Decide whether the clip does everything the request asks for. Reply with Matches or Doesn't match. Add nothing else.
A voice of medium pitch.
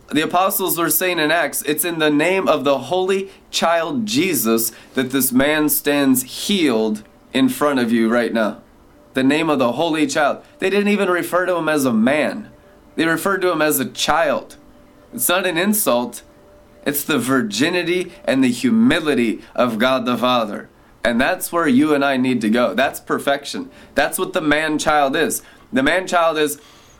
Matches